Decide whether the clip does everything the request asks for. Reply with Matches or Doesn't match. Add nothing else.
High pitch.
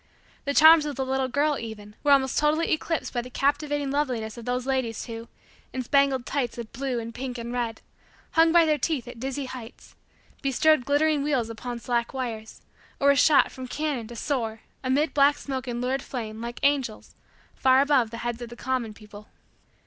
Matches